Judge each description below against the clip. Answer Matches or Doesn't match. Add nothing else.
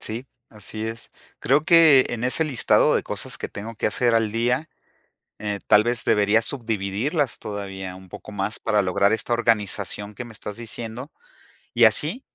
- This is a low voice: Matches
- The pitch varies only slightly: Doesn't match